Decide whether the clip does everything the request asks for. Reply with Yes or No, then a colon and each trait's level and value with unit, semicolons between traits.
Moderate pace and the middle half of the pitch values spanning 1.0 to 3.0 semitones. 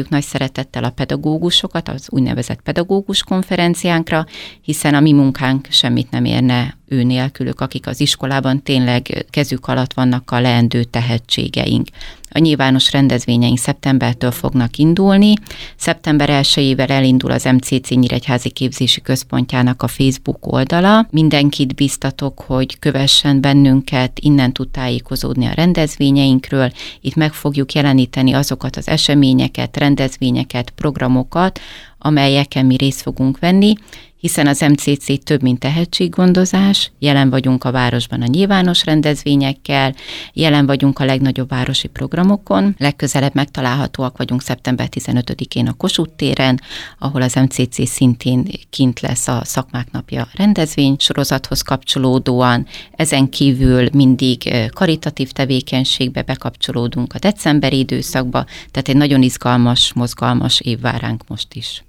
Yes: average, 120 wpm; narrow, 2.5 semitones